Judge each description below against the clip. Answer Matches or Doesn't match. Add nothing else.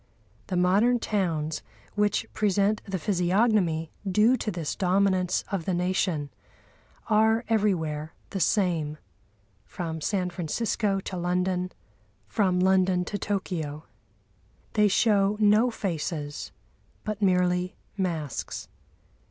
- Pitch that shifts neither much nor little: Matches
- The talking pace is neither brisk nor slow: Doesn't match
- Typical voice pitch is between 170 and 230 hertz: Matches